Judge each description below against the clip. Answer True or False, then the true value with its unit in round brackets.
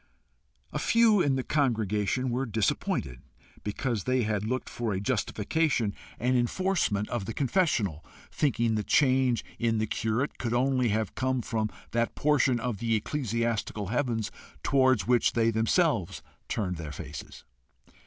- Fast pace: False (145 wpm)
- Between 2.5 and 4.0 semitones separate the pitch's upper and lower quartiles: True (3.5 semitones)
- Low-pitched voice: True (115 Hz)